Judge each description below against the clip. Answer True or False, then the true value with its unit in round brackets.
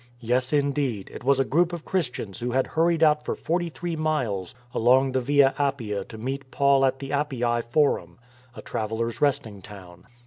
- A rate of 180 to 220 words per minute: True (185 wpm)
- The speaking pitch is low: True (130 Hz)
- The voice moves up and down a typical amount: True (3.8 semitones)